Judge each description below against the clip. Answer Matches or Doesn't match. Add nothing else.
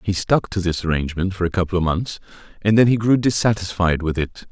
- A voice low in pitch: Matches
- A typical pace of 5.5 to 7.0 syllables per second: Matches